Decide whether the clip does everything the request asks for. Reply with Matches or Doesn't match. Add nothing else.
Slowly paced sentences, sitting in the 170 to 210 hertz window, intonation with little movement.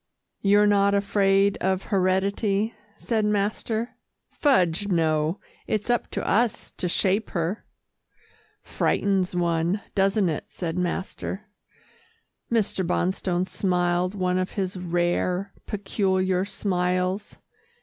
Matches